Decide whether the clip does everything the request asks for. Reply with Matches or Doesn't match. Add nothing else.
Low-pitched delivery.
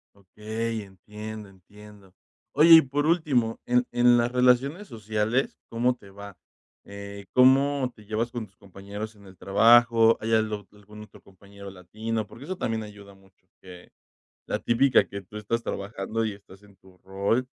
Matches